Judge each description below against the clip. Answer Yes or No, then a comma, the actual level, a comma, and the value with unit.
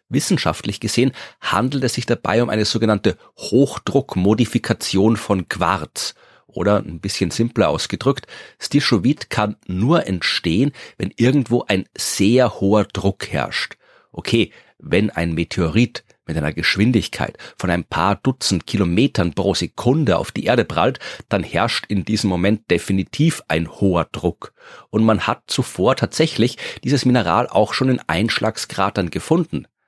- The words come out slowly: No, average, 135 wpm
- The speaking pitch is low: Yes, low, 105 Hz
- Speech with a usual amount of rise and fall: Yes, average, 4.1 semitones